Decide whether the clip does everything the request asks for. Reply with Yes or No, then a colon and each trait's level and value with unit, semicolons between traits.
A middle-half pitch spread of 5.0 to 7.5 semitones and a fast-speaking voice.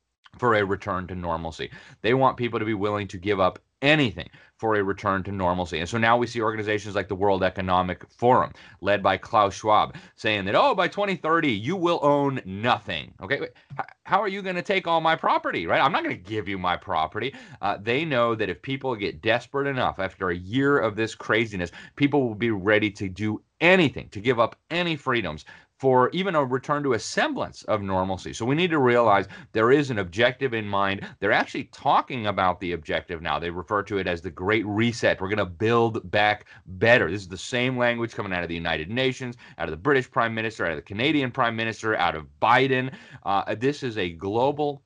Yes: average, 5.3 semitones; fast, 215 wpm